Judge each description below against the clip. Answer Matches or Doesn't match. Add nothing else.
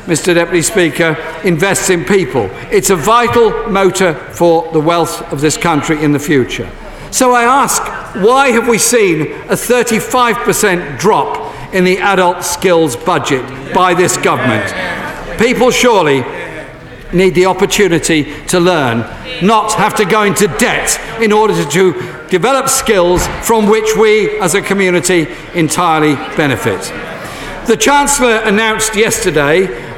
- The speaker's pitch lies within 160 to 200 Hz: Matches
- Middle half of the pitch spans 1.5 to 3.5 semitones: Doesn't match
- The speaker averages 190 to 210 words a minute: Doesn't match